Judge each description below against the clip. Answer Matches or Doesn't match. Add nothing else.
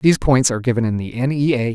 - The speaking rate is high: Matches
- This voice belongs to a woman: Doesn't match